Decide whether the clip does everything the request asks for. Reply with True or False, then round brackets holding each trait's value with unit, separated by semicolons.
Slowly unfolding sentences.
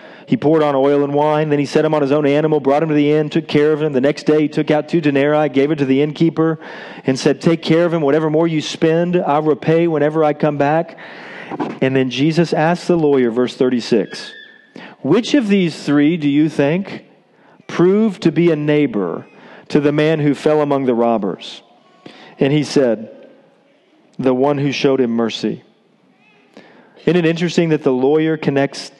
False (200 wpm)